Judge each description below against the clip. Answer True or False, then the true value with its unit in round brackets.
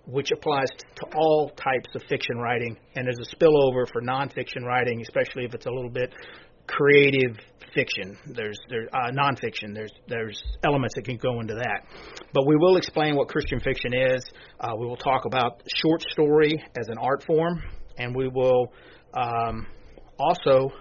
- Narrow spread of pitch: False (3.4 semitones)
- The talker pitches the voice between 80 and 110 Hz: False (130 Hz)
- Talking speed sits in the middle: True (170 wpm)